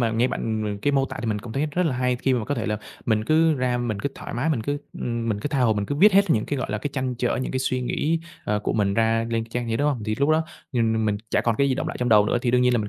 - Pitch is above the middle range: No, low, 120 Hz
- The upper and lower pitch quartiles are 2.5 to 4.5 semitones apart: Yes, average, 3.9 semitones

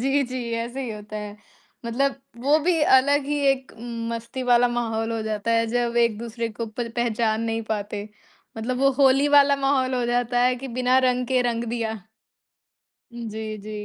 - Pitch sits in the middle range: No, high, 240 Hz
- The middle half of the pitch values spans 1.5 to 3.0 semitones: Yes, narrow, 2.4 semitones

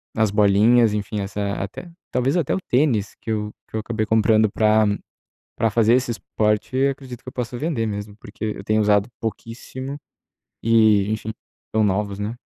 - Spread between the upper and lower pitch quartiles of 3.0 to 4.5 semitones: No, narrow, 2.5 semitones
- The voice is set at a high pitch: No, low, 110 Hz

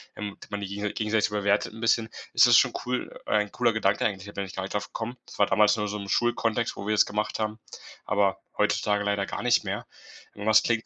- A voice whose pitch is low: Yes, low, 105 Hz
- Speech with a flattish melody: Yes, narrow, 1.4 semitones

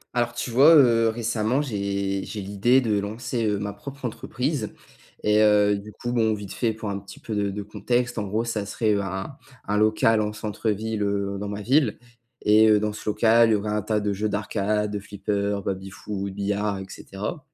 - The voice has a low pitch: Yes, low, 105 Hz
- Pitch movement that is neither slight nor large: No, narrow, 1.9 semitones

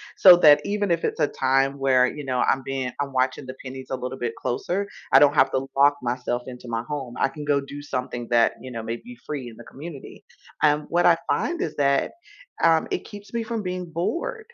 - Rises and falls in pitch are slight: No, average, 4.7 semitones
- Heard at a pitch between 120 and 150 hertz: Yes, medium, 140 Hz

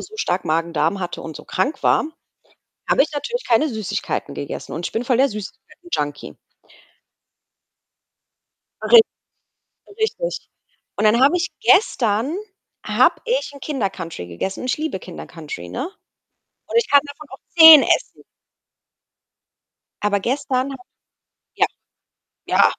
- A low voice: No, very high, 255 Hz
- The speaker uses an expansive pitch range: Yes, wide, 8.1 semitones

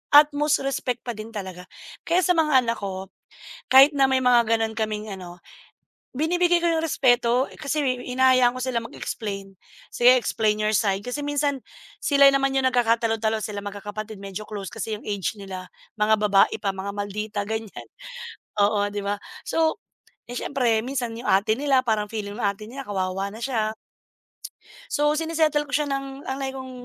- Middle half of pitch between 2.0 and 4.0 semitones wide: No, average, 4.8 semitones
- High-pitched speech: Yes, high, 230 Hz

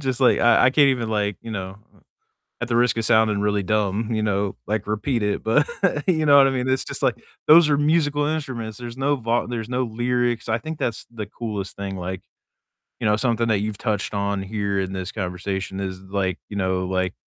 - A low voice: Yes, low, 110 Hz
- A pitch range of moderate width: Yes, average, 3.8 semitones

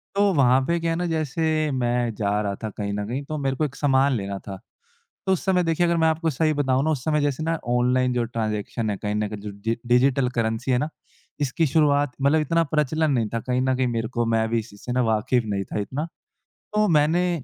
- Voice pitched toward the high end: No, low, 130 Hz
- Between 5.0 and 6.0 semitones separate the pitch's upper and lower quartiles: Yes, wide, 5.4 semitones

